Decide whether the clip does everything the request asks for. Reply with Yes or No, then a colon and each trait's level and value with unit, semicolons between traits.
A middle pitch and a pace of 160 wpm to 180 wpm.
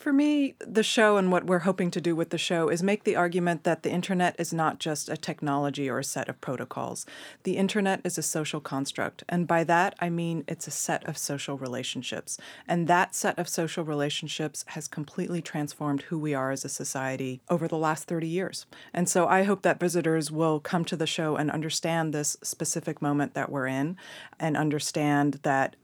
No: medium, 165 Hz; fast, 205 wpm